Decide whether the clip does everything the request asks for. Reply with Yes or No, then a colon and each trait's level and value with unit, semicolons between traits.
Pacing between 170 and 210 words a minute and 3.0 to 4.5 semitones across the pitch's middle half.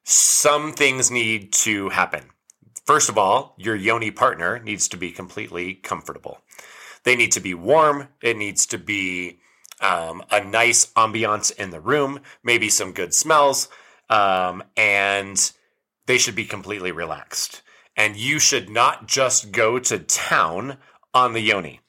No: average, 150 wpm; average, 3.8 semitones